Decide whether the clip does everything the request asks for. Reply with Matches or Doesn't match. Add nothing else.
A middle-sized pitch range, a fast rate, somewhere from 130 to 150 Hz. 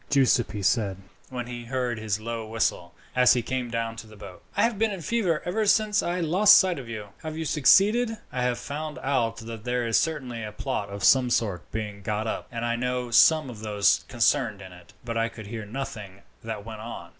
Doesn't match